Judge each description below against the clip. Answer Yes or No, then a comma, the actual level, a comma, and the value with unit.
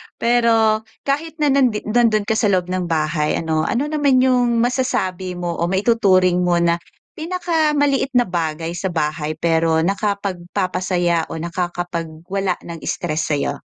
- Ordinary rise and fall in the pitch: No, wide, 6.0 semitones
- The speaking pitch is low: No, medium, 185 Hz